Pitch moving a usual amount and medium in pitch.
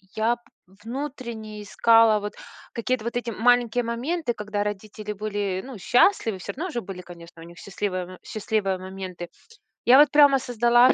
No: average, 3.7 semitones; high, 220 Hz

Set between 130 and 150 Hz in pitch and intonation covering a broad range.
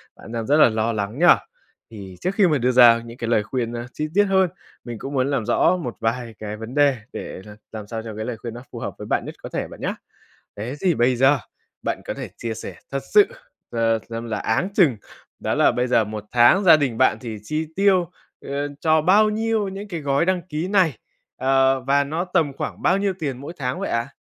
Yes: low, 135 Hz; wide, 6.4 semitones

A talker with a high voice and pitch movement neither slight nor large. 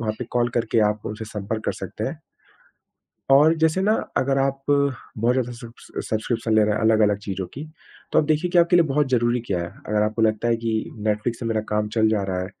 No: low, 115 Hz; average, 4.0 semitones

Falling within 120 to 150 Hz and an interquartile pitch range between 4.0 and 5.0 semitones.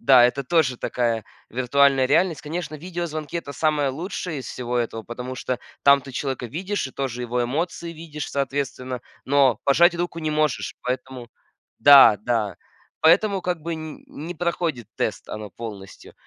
Yes: medium, 140 Hz; average, 4.6 semitones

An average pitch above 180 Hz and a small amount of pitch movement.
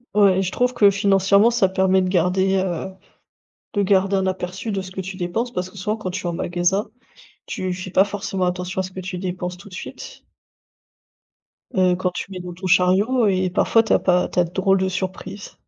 Yes: high, 190 Hz; narrow, 1.5 semitones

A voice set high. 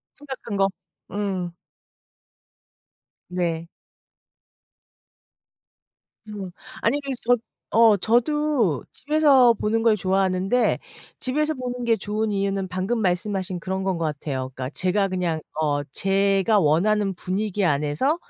Yes: high, 195 Hz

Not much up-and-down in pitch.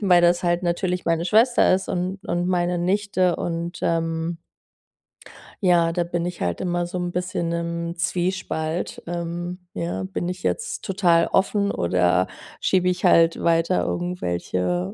Yes: narrow, 1.4 semitones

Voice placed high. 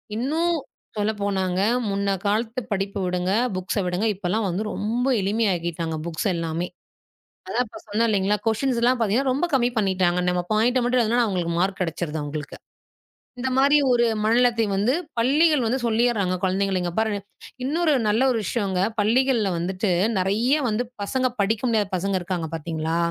Yes: high, 205 Hz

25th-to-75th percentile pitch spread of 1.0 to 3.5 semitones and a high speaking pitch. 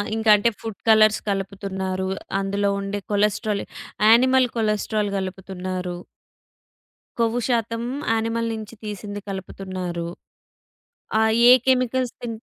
Yes: average, 2.9 semitones; high, 210 Hz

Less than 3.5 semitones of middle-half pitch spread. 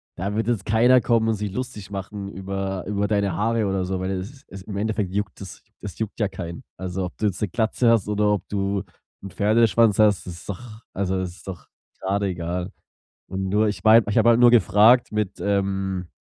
Yes: narrow, 2.4 semitones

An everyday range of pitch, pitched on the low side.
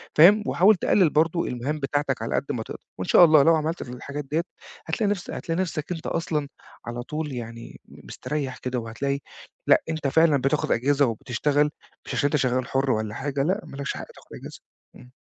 No: average, 4.0 semitones; medium, 145 Hz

